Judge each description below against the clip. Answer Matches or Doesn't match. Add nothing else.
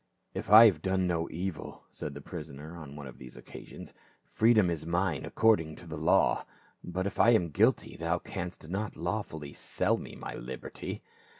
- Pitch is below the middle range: Matches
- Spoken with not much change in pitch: Doesn't match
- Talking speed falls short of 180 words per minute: Doesn't match